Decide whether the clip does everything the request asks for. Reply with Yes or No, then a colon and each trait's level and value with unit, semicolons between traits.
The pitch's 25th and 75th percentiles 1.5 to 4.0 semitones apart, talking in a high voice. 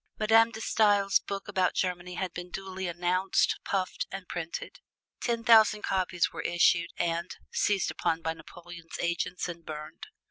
No: narrow, 2.6 semitones; medium, 180 Hz